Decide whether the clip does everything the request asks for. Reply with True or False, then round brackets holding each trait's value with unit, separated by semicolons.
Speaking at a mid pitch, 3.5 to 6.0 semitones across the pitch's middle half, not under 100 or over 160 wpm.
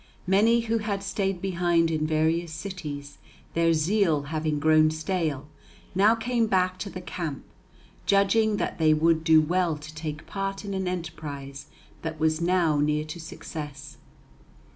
True (165 Hz; 3.8 semitones; 150 wpm)